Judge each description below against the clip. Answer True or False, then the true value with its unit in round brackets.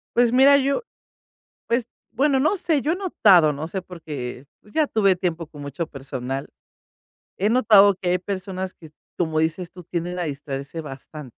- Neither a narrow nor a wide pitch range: False (6.7 semitones)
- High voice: False (180 Hz)